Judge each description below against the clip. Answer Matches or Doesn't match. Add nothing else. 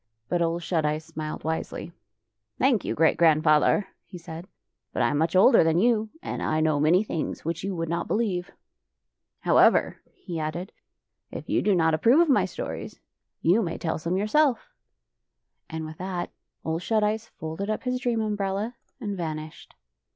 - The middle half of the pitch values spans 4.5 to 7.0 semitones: Matches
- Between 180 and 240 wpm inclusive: Matches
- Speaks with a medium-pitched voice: Matches